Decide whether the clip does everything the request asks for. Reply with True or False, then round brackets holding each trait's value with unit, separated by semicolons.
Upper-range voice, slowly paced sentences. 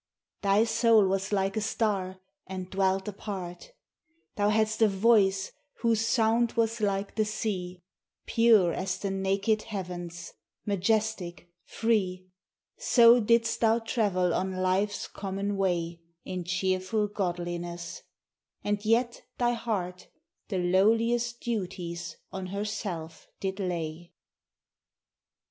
True (195 Hz; 115 wpm)